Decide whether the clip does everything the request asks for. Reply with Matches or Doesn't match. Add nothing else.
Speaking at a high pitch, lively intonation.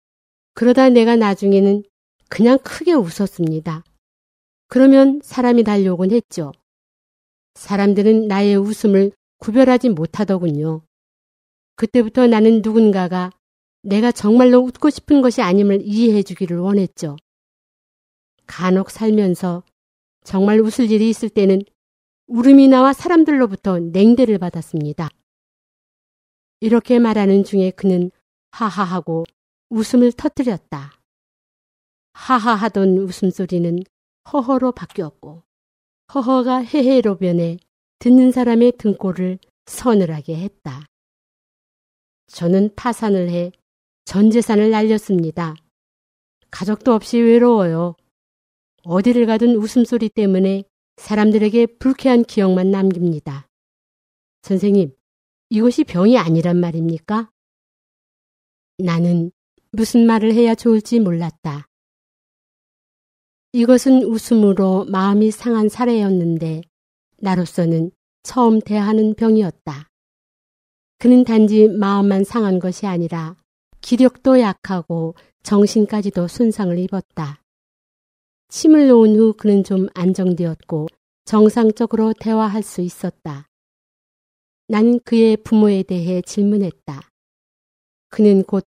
Doesn't match